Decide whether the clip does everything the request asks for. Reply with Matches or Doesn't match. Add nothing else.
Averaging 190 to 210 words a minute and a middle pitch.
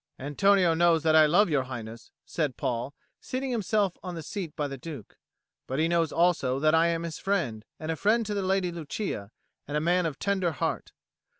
Matches